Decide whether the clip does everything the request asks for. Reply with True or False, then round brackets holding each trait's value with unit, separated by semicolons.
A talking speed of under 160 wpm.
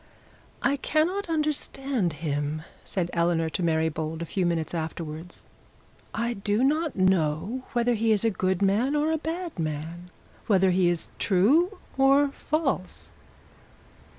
True (140 wpm)